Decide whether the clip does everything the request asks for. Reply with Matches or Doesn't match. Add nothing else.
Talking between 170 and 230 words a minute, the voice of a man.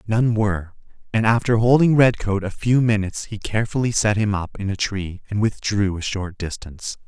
Matches